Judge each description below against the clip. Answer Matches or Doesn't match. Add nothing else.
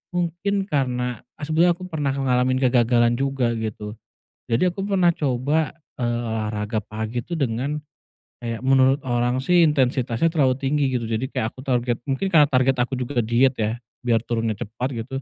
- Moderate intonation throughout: Matches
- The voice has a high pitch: Doesn't match